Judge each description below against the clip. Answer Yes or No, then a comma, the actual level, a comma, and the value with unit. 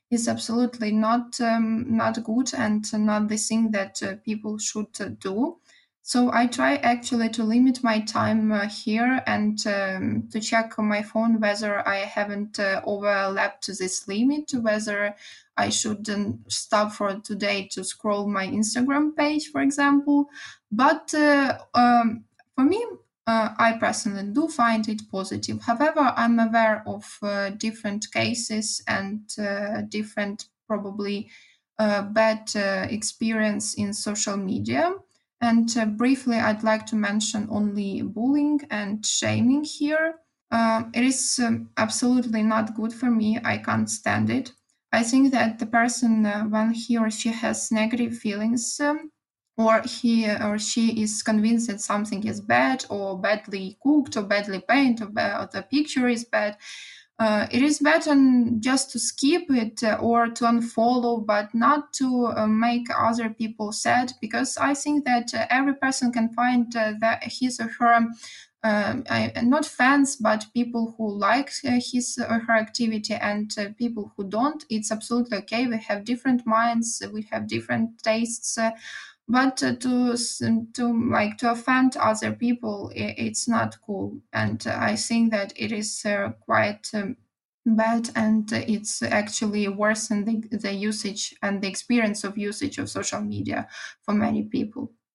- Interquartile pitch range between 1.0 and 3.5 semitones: Yes, narrow, 2.4 semitones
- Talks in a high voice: Yes, high, 225 Hz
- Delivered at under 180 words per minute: Yes, average, 155 wpm